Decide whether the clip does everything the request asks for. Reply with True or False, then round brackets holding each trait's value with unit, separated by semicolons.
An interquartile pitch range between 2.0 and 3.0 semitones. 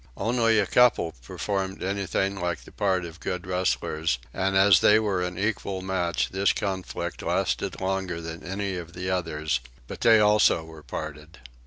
True (2.7 semitones)